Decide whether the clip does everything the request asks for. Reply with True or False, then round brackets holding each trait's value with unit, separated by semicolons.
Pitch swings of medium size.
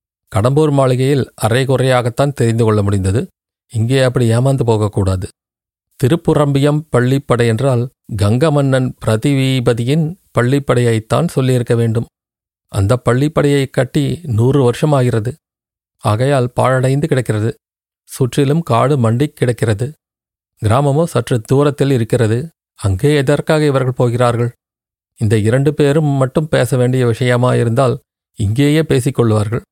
True (3.4 semitones)